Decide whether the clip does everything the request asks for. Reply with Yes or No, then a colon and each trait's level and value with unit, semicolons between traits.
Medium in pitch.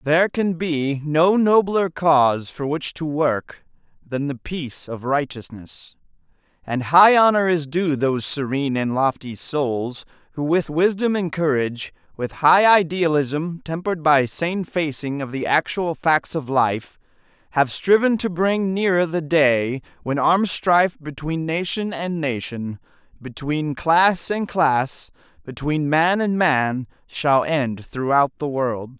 Yes: medium, 155 Hz